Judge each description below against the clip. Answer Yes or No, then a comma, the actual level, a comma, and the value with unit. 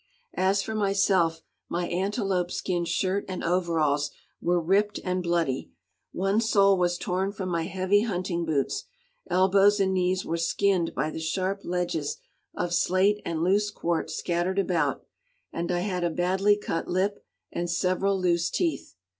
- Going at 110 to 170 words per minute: Yes, average, 155 wpm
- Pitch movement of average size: No, narrow, 2.3 semitones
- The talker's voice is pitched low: No, medium, 185 Hz